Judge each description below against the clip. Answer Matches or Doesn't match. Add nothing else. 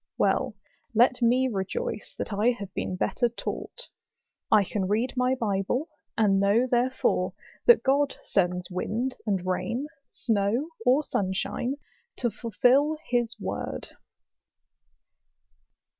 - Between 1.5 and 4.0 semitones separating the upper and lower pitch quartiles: Doesn't match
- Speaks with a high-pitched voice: Matches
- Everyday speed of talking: Doesn't match